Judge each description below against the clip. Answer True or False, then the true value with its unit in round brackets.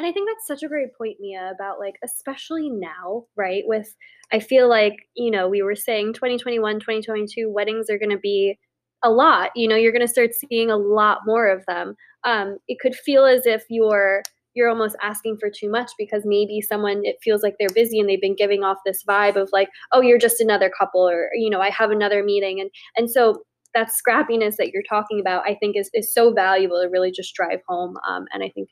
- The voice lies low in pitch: False (210 Hz)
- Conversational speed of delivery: False (230 wpm)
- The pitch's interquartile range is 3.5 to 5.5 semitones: False (2.5 semitones)